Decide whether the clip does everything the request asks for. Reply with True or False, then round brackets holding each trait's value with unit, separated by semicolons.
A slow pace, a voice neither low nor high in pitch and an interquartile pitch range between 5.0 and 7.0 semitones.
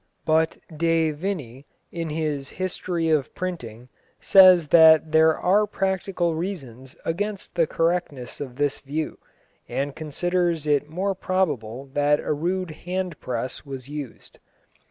False (130 wpm; 160 Hz; 3.9 semitones)